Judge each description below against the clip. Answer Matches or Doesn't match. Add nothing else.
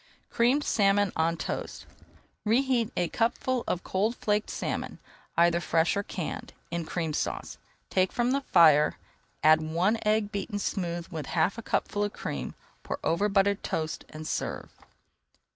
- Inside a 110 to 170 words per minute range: Matches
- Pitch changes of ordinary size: Matches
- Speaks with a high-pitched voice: Matches